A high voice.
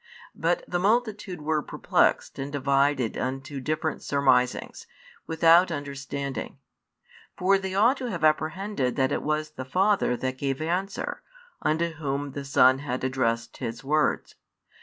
No: medium, 145 Hz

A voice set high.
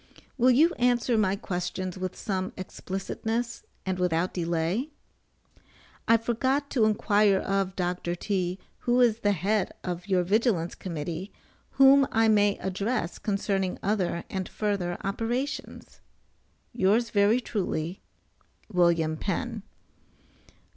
Yes: high, 195 Hz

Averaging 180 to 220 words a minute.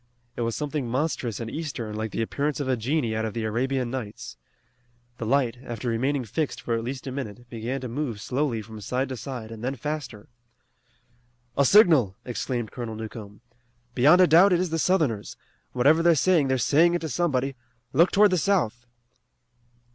Yes: average, 185 wpm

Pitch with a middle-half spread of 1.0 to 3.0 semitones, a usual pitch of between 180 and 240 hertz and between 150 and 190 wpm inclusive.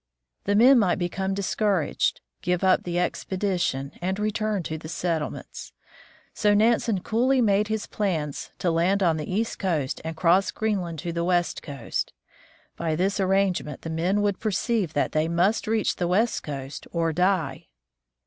No: average, 3.9 semitones; medium, 185 Hz; average, 160 wpm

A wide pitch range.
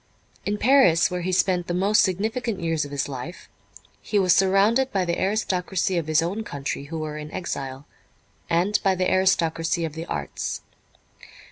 No: average, 3.4 semitones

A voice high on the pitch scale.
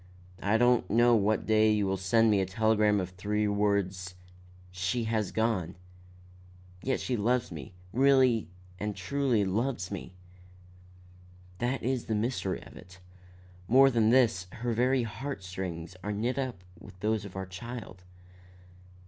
No: low, 105 Hz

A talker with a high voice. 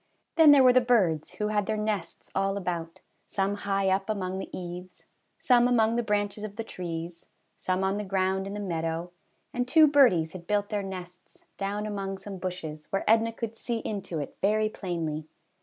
Yes: high, 195 Hz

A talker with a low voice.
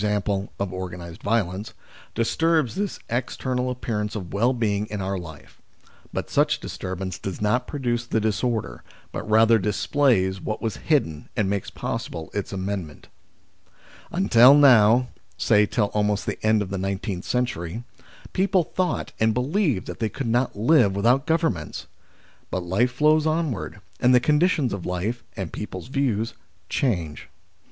Yes: low, 110 Hz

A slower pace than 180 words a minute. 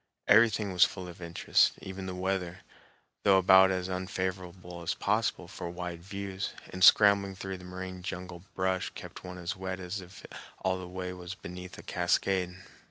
Yes: average, 170 wpm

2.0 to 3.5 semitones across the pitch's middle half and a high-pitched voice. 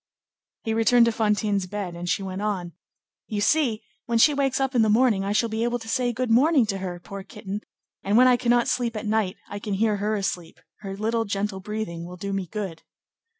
Yes: average, 3.1 semitones; high, 215 Hz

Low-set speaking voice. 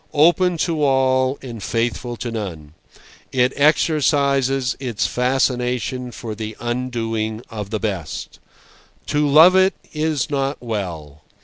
Yes: low, 125 Hz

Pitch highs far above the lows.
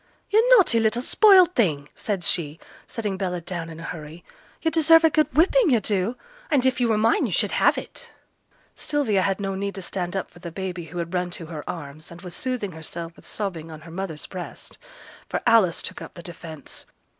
Yes: wide, 5.9 semitones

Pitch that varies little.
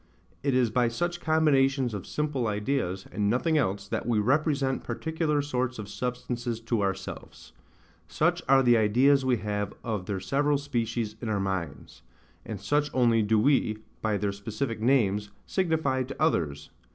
No: average, 4.9 semitones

